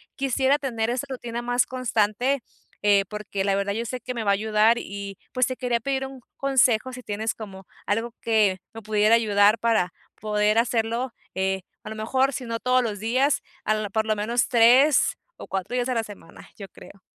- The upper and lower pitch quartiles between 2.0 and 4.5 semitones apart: Yes, average, 3.2 semitones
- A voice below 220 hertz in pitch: No, high, 225 Hz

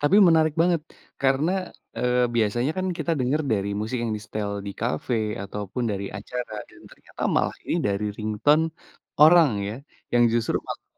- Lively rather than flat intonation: Yes, wide, 5.8 semitones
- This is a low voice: Yes, low, 125 Hz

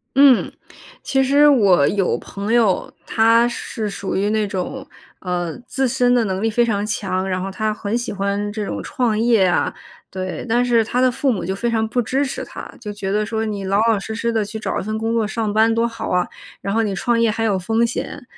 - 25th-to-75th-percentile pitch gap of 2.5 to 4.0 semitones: Yes, average, 2.8 semitones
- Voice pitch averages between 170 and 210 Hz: No, high, 220 Hz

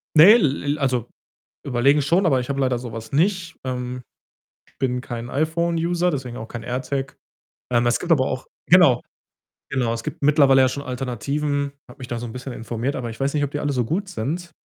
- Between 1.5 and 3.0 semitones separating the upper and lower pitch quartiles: No, average, 3.4 semitones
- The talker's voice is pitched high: No, low, 135 Hz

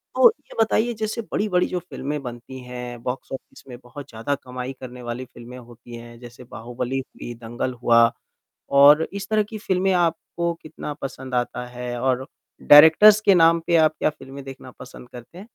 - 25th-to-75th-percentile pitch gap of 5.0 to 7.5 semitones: Yes, wide, 5.4 semitones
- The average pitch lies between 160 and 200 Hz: No, low, 130 Hz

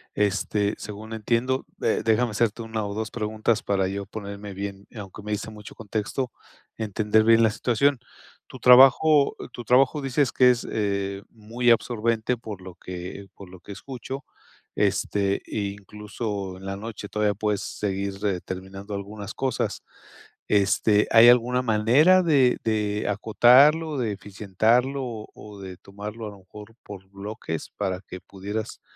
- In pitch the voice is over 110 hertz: No, low, 105 Hz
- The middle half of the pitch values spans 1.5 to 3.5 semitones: Yes, average, 2.9 semitones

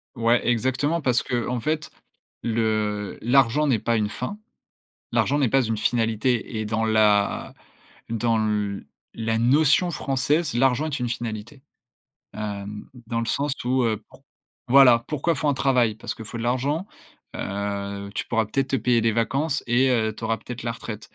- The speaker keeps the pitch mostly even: No, average, 3.3 semitones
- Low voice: Yes, low, 115 Hz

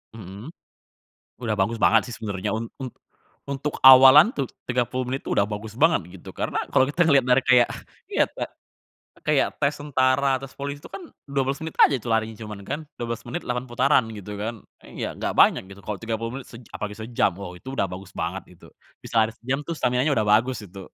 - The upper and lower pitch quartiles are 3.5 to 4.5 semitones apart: Yes, average, 4.1 semitones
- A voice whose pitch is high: No, low, 120 Hz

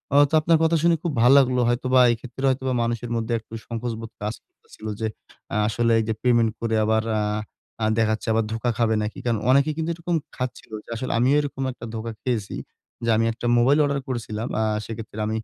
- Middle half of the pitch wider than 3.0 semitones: No, narrow, 2.6 semitones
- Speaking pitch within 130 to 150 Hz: No, low, 120 Hz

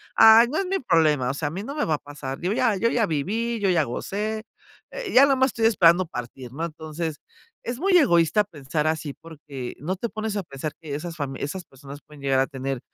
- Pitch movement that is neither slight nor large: No, wide, 7.4 semitones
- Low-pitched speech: No, medium, 165 Hz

